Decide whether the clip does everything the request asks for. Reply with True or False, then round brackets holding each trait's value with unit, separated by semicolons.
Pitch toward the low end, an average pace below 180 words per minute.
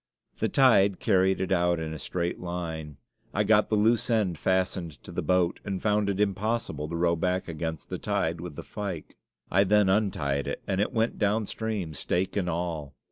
False (95 Hz; 190 wpm)